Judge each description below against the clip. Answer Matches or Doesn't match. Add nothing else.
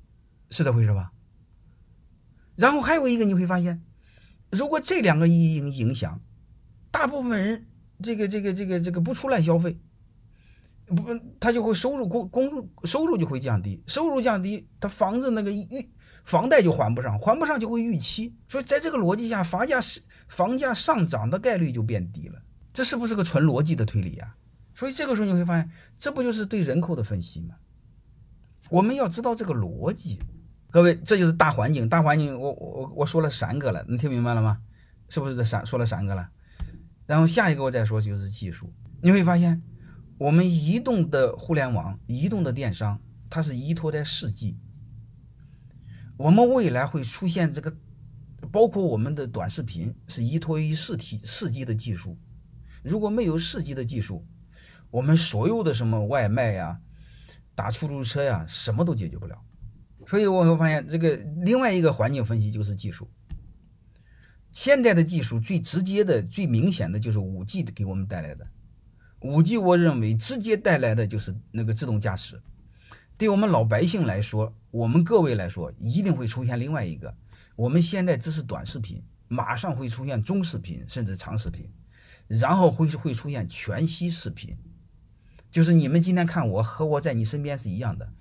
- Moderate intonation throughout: Doesn't match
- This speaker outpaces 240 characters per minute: Matches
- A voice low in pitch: Doesn't match